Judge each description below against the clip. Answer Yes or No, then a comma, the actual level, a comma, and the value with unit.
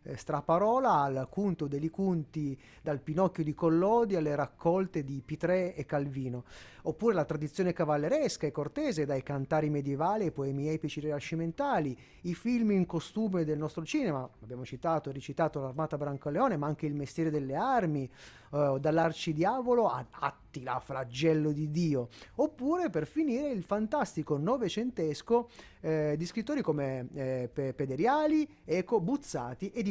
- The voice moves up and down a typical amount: Yes, average, 4.9 semitones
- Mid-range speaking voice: Yes, medium, 155 Hz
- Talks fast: No, average, 145 wpm